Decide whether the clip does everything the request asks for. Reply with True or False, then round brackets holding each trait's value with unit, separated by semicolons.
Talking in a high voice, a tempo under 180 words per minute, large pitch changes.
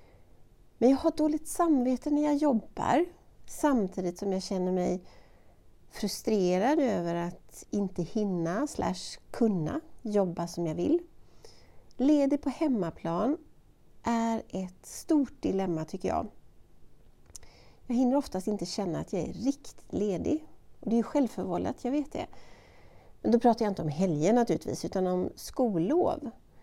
True (225 Hz; 135 wpm; 7.7 semitones)